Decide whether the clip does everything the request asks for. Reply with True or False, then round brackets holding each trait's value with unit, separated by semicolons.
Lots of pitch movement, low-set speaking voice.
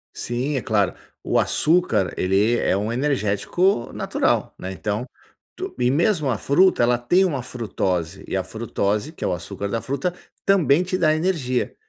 True (7.2 semitones; 125 Hz)